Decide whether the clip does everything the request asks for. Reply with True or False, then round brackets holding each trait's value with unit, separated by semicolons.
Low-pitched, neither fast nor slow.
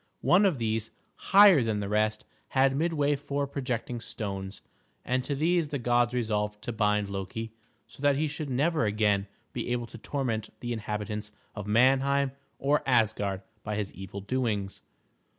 True (120 Hz; 160 wpm)